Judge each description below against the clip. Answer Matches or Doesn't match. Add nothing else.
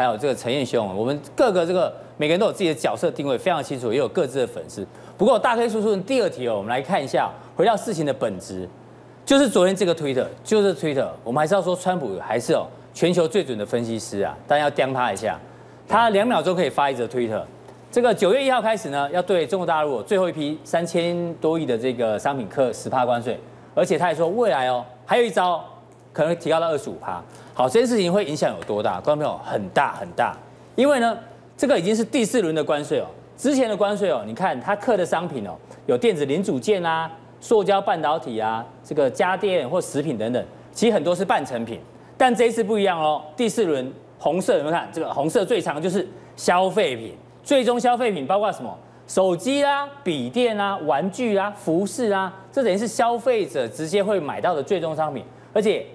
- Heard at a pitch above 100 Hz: Matches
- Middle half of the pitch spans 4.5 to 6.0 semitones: Doesn't match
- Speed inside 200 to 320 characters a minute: Doesn't match